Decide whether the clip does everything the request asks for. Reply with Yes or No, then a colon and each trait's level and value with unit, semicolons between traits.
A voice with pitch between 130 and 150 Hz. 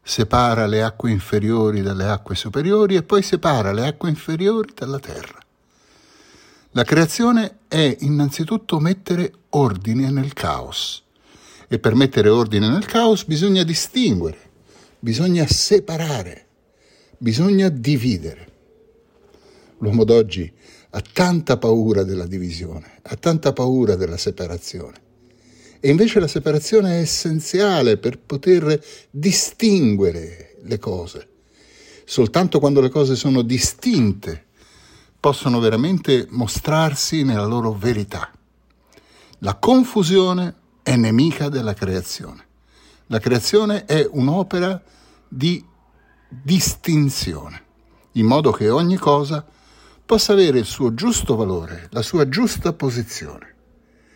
Yes: medium, 140 Hz